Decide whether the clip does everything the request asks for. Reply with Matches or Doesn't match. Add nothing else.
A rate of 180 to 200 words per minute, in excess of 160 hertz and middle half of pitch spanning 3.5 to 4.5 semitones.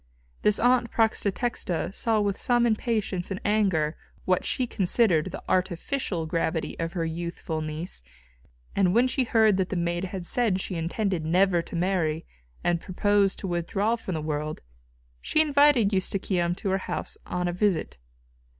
Doesn't match